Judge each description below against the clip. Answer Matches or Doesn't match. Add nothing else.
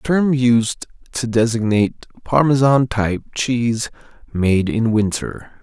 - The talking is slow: Matches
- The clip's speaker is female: Doesn't match